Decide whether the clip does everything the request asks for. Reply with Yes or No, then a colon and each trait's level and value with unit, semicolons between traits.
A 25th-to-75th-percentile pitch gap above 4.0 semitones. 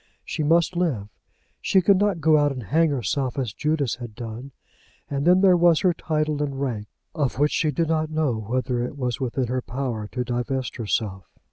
Yes: average, 4.4 semitones